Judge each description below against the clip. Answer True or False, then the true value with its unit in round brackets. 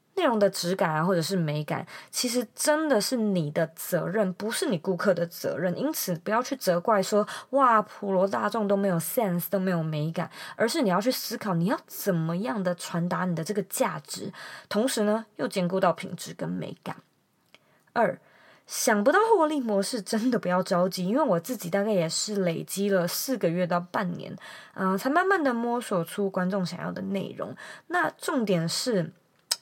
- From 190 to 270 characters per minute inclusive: False (280 characters per minute)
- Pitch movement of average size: True (4.3 semitones)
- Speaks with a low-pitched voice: False (195 Hz)